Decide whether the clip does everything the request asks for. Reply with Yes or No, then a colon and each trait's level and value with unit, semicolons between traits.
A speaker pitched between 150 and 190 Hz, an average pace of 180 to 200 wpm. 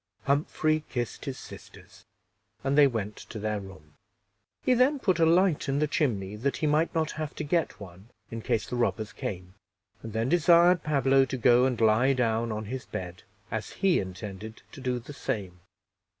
No: low, 125 Hz; average, 185 wpm